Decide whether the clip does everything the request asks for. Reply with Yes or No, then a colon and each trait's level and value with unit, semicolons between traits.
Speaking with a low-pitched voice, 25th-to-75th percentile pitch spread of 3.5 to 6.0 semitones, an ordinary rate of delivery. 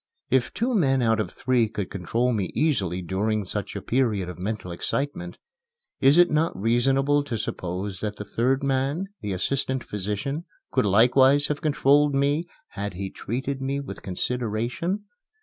Yes: low, 125 Hz; average, 5.3 semitones; average, 160 wpm